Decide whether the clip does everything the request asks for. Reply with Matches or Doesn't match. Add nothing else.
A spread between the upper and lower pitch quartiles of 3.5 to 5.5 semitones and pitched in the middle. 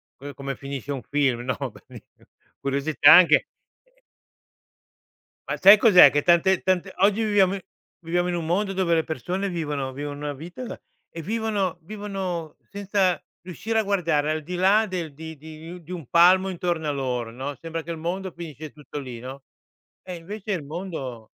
Matches